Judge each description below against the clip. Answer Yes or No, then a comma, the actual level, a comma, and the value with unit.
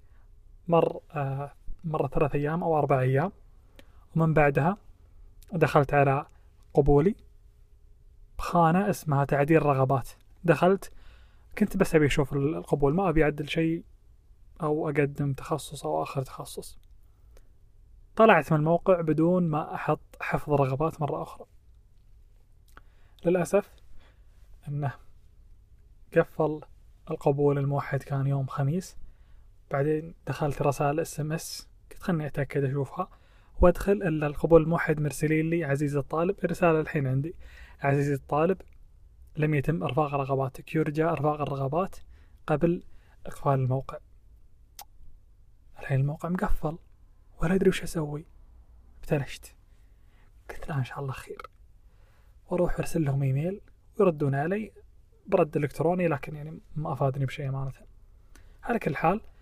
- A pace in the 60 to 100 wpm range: No, average, 115 wpm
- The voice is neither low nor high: Yes, medium, 145 Hz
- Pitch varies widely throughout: Yes, wide, 7.9 semitones